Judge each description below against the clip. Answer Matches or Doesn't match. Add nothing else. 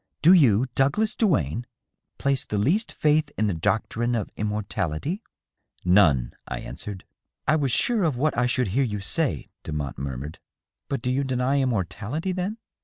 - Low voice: Matches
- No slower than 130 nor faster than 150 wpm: Doesn't match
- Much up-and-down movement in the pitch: Matches